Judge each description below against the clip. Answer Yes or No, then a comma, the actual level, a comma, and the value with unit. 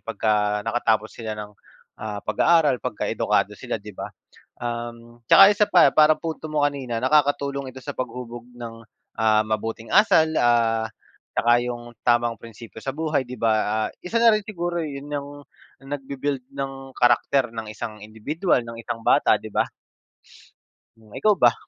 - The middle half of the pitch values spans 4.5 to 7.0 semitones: No, average, 4.1 semitones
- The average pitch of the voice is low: Yes, low, 120 Hz